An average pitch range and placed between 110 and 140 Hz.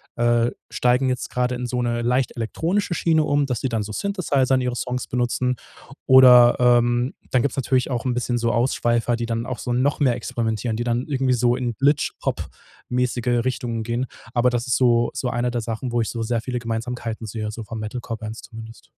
No: narrow, 1.4 semitones; low, 120 Hz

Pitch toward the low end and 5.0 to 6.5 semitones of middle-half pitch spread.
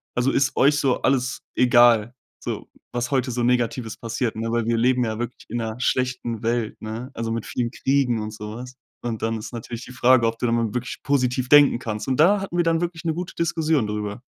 No: low, 120 Hz; narrow, 2.5 semitones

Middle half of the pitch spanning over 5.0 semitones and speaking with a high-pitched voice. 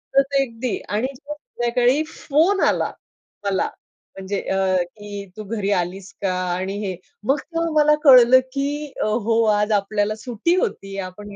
Yes: wide, 5.6 semitones; high, 225 Hz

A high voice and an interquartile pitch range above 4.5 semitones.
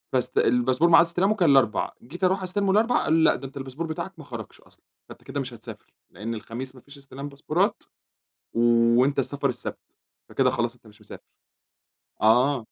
No: low, 135 Hz; wide, 5.4 semitones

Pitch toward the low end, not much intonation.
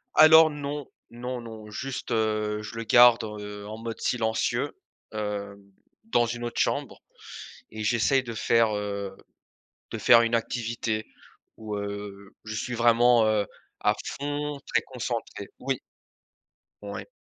Yes: low, 115 Hz; narrow, 2.3 semitones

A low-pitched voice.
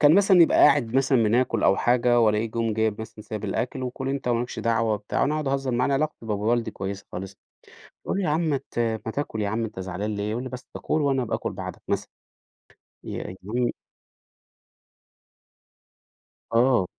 Yes: low, 120 Hz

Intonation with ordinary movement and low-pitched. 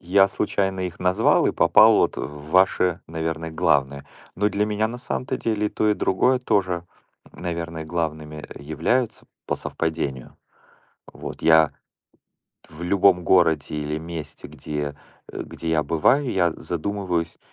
Yes: average, 3.9 semitones; very low, 85 Hz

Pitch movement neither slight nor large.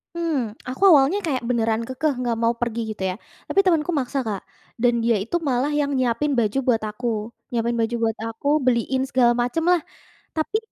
Yes: average, 3.9 semitones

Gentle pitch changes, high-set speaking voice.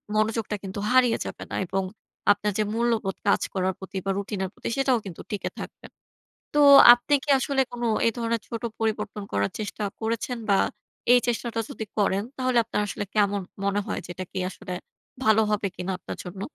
No: average, 3.1 semitones; high, 215 Hz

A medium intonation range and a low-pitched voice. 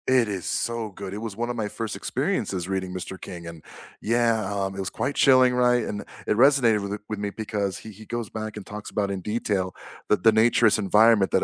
Yes: average, 3.0 semitones; low, 105 Hz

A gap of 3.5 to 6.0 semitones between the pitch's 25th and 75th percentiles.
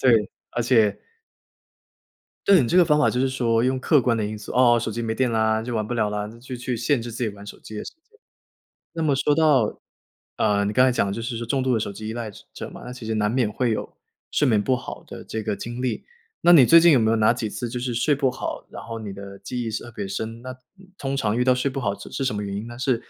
No: average, 3.0 semitones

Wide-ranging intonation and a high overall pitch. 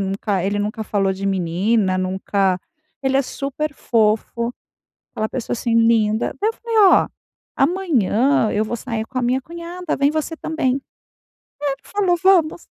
Yes: wide, 6.6 semitones; high, 235 Hz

